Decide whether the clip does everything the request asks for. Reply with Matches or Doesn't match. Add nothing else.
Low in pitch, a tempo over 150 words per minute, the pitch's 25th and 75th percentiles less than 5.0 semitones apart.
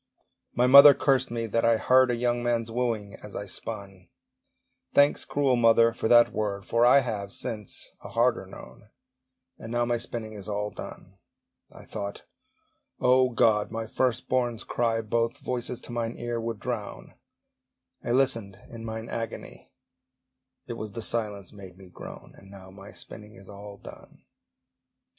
Matches